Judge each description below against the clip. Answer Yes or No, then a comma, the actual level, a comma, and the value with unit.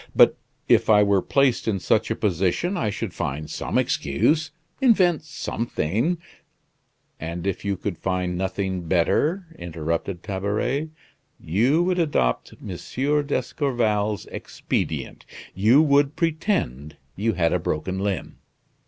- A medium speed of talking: No, slow, 125 wpm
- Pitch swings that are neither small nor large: No, wide, 8.4 semitones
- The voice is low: Yes, low, 105 Hz